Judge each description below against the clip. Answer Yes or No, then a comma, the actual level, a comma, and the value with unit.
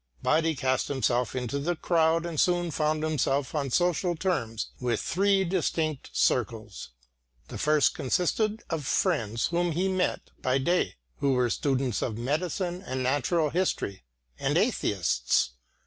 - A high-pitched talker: No, medium, 155 Hz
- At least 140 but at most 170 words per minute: Yes, average, 145 wpm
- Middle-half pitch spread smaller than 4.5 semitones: No, average, 5.2 semitones